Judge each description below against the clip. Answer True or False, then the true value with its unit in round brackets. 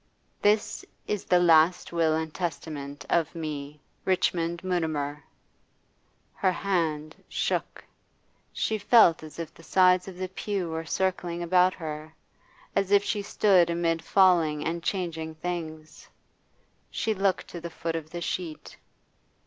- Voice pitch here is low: False (170 Hz)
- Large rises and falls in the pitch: False (2.7 semitones)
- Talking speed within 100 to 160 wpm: True (140 wpm)